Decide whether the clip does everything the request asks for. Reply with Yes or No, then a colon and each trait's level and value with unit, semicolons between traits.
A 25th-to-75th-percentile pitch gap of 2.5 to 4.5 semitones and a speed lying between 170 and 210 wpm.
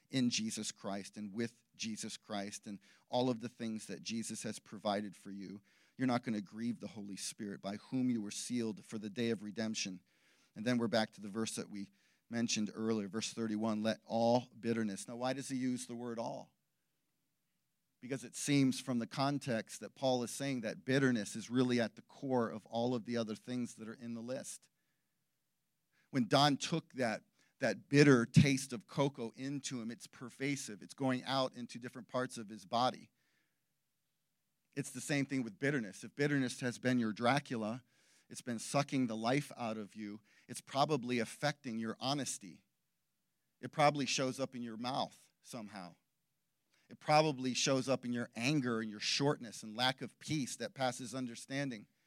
Yes: average, 3.0 semitones; average, 185 wpm